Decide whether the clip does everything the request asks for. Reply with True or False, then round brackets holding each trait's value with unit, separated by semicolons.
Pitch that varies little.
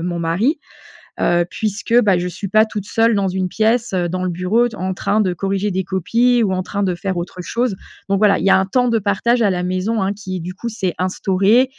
False (3.1 semitones)